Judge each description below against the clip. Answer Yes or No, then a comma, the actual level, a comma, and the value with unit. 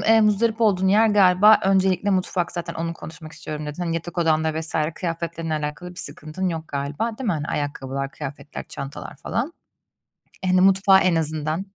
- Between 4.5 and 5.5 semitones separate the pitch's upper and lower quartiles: No, average, 3.7 semitones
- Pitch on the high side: No, medium, 170 Hz